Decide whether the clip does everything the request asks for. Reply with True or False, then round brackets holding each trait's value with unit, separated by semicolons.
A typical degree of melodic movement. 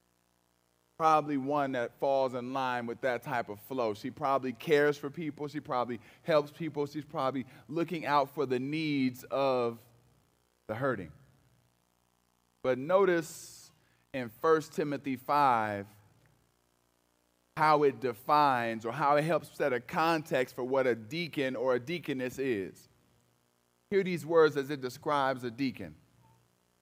False (6.8 semitones)